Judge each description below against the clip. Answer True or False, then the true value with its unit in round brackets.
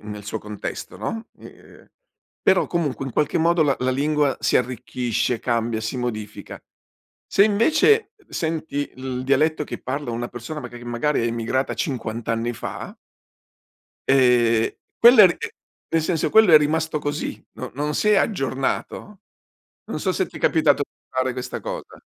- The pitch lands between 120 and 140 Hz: True (135 Hz)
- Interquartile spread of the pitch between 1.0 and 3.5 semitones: False (5.0 semitones)